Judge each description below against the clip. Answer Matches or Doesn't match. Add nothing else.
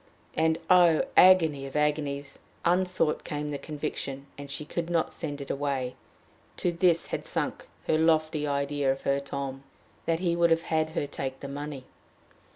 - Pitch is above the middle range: Doesn't match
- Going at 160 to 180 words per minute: Matches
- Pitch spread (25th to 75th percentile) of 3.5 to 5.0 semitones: Doesn't match